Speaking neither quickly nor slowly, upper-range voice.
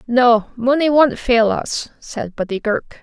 Yes: average, 160 wpm; high, 240 Hz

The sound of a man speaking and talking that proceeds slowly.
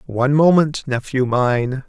Yes: male; slow, 130 wpm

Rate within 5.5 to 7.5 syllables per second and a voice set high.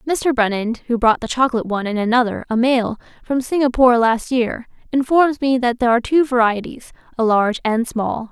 Yes: 5.8 syllables/s; high, 240 Hz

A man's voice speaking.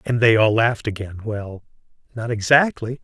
Yes: male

